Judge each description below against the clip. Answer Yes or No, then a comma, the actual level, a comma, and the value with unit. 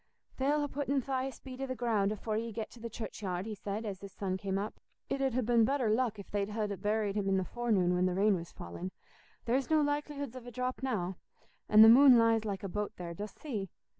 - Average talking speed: No, fast, 245 wpm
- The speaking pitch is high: Yes, high, 220 Hz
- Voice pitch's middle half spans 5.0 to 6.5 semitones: No, average, 4.4 semitones